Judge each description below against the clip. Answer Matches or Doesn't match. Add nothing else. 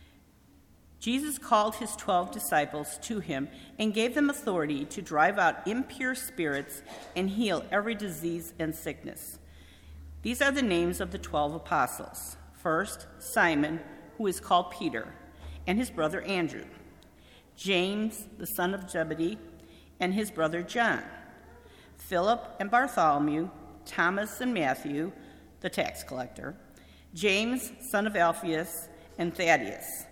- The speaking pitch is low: Doesn't match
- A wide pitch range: Matches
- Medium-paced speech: Doesn't match